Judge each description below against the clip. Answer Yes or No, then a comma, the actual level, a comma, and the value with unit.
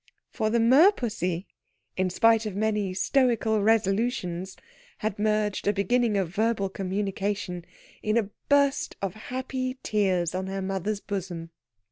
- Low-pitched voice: No, high, 205 Hz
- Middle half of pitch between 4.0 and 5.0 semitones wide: No, average, 3.0 semitones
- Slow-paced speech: Yes, slow, 130 wpm